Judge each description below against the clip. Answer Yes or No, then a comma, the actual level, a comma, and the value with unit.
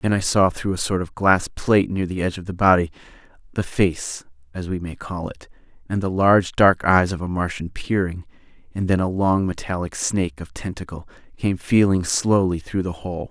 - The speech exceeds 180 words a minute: Yes, fast, 205 wpm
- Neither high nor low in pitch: No, very low, 90 Hz